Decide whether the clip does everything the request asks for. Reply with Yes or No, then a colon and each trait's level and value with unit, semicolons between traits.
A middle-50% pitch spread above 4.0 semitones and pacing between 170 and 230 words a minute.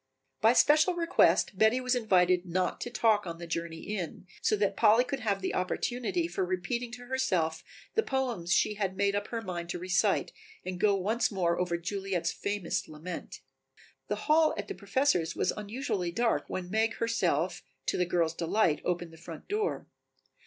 Yes: average, 5.1 semitones; average, 180 wpm